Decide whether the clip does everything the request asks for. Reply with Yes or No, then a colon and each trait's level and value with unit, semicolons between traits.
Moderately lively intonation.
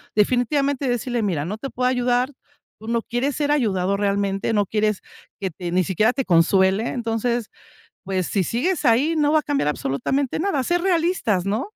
No: wide, 5.8 semitones